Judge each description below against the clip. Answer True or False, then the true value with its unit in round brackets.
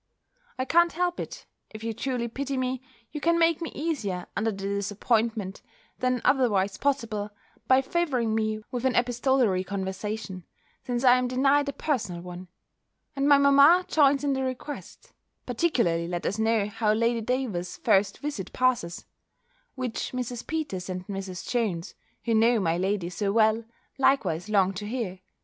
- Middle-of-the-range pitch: False (230 Hz)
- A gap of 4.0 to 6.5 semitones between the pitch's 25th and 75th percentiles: True (5.1 semitones)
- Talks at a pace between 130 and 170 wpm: True (160 wpm)